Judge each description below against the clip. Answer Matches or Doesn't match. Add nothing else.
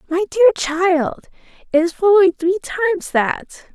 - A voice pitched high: Matches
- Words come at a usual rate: Doesn't match